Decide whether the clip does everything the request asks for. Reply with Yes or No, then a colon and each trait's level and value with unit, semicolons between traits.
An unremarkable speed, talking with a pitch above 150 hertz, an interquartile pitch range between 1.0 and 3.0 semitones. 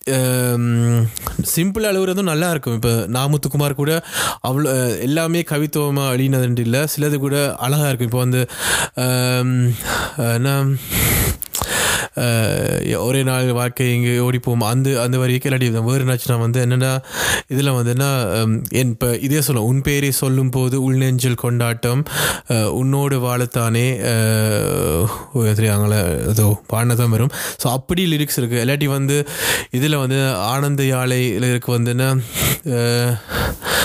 No: average, 110 wpm; low, 125 Hz; narrow, 2.5 semitones